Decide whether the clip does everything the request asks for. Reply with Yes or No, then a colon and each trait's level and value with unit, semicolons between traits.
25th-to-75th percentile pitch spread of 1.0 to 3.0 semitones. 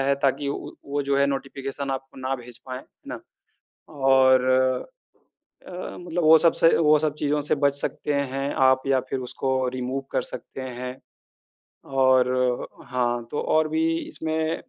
Yes: narrow, 2.4 semitones